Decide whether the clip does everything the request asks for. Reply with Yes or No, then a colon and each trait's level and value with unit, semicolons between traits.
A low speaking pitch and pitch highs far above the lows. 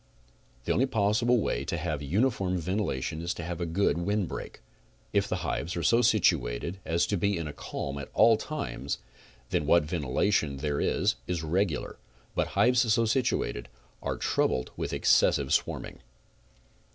Yes: very low, 85 Hz; wide, 5.8 semitones